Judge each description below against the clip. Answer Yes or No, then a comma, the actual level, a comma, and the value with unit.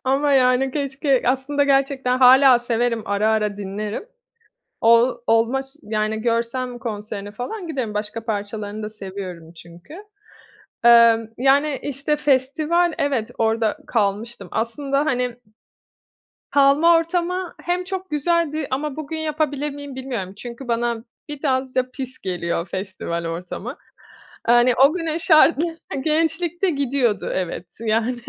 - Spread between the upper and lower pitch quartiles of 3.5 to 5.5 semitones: Yes, average, 4.8 semitones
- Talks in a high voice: Yes, very high, 255 Hz